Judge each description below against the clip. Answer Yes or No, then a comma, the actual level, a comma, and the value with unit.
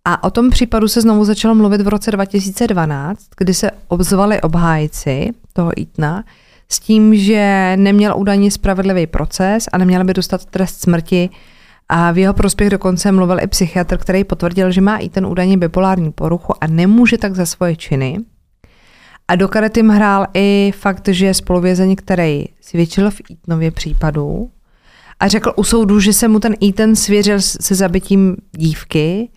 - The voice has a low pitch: No, high, 195 Hz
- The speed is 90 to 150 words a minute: No, average, 165 wpm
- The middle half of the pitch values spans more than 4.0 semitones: No, narrow, 2.5 semitones